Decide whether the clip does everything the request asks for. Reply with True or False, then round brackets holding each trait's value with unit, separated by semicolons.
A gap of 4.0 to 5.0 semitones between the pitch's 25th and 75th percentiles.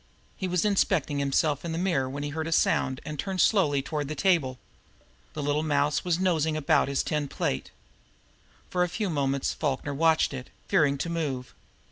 False (3.3 semitones)